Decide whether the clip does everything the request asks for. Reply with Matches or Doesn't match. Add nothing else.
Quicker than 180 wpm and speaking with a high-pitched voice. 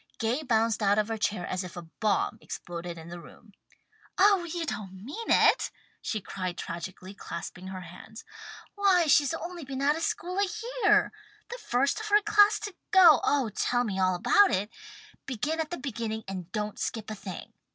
Matches